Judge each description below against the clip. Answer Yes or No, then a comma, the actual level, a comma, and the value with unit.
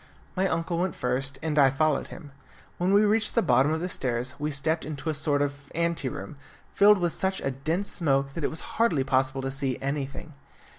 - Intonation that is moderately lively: Yes, average, 3.8 semitones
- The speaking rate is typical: No, fast, 210 wpm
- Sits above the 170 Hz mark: No, medium, 150 Hz